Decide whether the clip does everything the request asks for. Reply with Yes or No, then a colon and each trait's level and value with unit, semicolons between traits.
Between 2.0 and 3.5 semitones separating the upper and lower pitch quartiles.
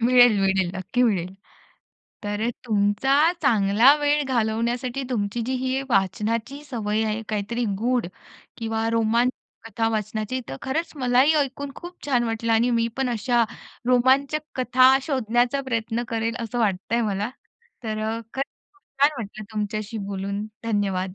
Yes: average, 3.1 semitones